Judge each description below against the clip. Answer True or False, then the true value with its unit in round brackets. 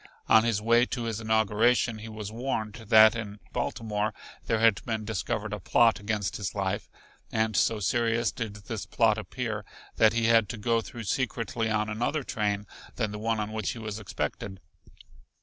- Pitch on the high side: False (110 Hz)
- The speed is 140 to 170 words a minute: False (180 wpm)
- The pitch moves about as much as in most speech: False (1.7 semitones)